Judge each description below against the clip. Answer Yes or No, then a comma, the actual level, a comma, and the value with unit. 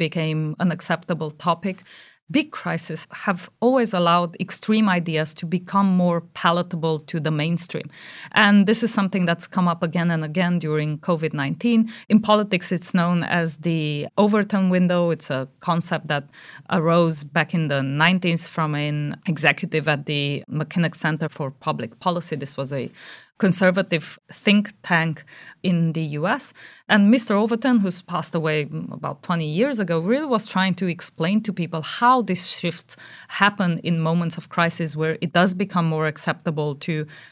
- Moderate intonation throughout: Yes, average, 3.0 semitones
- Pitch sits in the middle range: Yes, medium, 170 Hz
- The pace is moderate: Yes, average, 160 wpm